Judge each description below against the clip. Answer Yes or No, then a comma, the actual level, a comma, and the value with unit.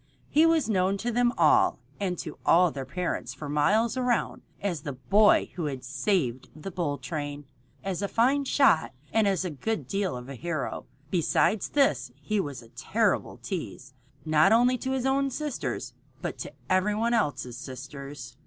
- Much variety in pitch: Yes, wide, 8.0 semitones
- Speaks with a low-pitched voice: No, medium, 180 Hz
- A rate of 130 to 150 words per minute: No, average, 175 wpm